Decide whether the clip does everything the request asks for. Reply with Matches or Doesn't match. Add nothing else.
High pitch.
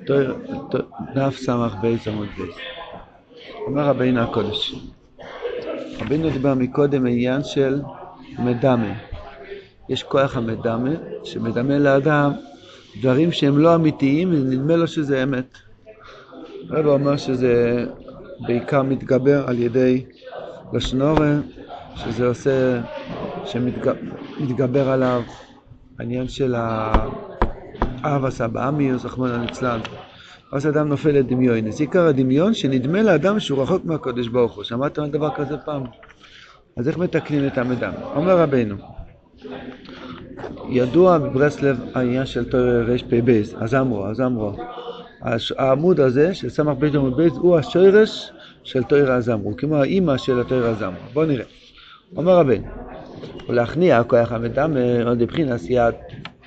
Doesn't match